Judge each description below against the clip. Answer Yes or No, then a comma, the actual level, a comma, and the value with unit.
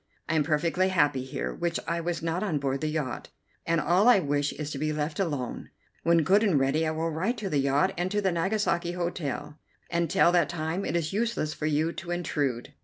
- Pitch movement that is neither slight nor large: Yes, average, 3.0 semitones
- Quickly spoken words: Yes, fast, 220 wpm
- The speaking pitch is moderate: Yes, medium, 165 Hz